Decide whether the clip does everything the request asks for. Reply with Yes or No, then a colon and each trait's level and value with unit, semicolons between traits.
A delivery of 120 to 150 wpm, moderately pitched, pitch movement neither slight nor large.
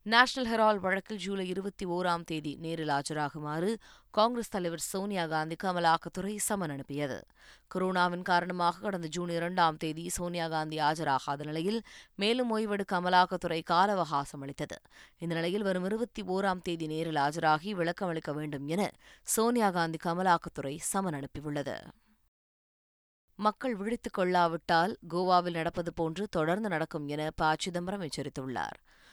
Yes: average, 125 wpm; medium, 175 Hz; average, 3.8 semitones